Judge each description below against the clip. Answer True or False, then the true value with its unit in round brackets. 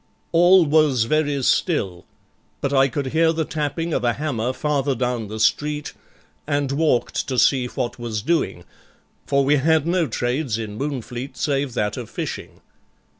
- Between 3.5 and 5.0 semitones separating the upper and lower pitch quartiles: True (3.9 semitones)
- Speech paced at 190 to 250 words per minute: False (160 wpm)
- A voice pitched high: False (140 Hz)